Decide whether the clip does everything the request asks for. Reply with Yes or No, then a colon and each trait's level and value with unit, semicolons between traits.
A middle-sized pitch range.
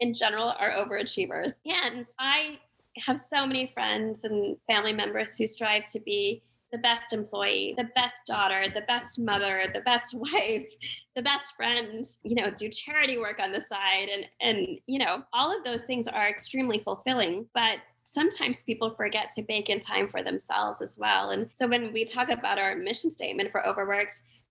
Yes: average, 3.3 semitones